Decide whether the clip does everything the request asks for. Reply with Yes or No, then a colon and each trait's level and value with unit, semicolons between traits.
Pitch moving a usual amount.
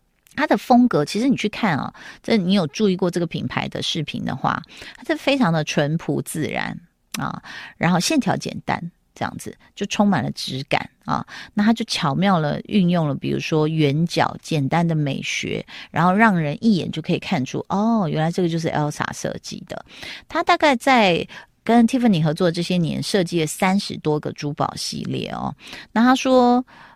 No: wide, 6.2 semitones